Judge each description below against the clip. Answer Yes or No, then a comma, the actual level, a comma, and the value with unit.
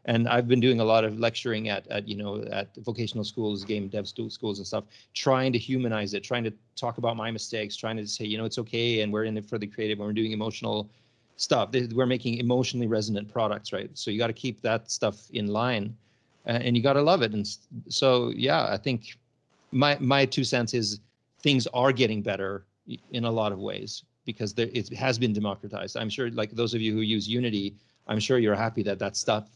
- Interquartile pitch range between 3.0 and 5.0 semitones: No, narrow, 2.4 semitones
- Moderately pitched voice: No, low, 115 Hz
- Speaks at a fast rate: Yes, fast, 225 wpm